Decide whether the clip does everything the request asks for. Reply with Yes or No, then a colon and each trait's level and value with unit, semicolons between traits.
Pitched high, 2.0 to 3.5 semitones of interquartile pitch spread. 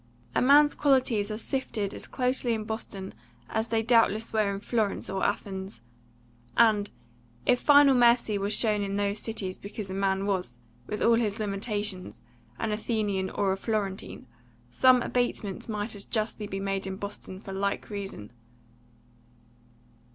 Yes: high, 210 Hz; narrow, 2.6 semitones